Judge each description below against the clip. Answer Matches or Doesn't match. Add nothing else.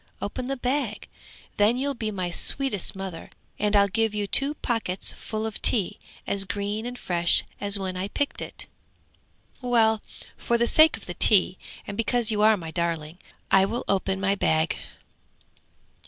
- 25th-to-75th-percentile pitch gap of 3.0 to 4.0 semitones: Matches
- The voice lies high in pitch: Matches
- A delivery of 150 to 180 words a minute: Matches